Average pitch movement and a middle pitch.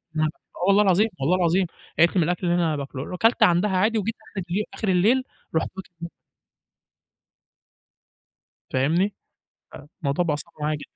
Yes: average, 3.6 semitones; medium, 175 Hz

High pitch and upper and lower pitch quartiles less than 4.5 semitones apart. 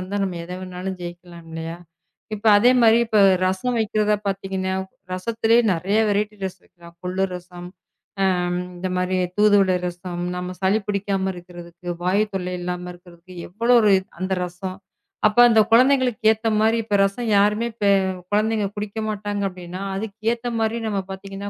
Yes: high, 195 Hz; average, 2.9 semitones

